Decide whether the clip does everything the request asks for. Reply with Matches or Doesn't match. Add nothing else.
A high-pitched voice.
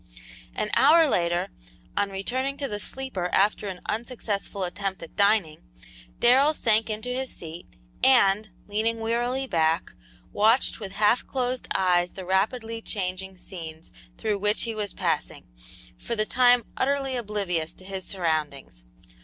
Matches